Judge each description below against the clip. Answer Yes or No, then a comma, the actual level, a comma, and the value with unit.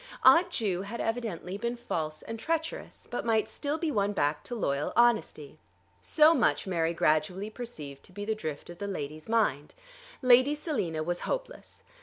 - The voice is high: Yes, high, 205 Hz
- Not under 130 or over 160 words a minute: No, average, 170 wpm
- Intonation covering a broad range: Yes, wide, 7.1 semitones